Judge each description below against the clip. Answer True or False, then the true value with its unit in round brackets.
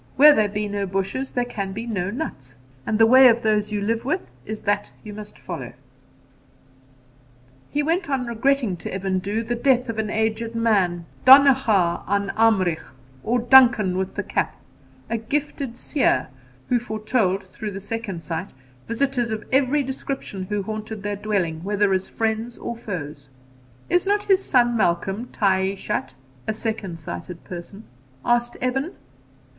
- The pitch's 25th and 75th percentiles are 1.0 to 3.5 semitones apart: False (3.9 semitones)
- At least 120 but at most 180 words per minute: True (160 wpm)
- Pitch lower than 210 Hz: False (220 Hz)